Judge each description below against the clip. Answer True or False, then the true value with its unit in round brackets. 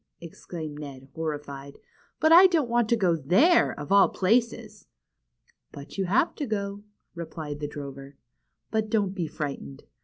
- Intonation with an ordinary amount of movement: False (7.0 semitones)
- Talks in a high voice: False (175 Hz)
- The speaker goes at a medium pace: True (150 wpm)